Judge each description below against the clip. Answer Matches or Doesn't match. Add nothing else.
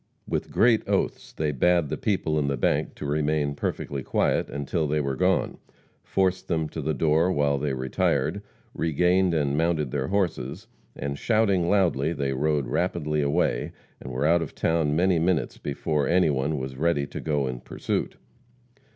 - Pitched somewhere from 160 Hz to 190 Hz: Doesn't match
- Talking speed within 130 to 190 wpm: Matches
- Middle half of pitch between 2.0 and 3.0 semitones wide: Doesn't match